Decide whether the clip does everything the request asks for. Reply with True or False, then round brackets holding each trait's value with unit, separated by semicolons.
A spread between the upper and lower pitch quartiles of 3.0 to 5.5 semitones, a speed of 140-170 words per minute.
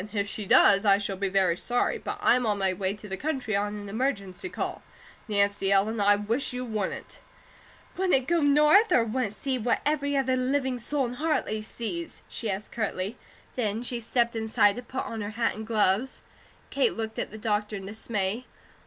False (4.0 semitones; 195 wpm)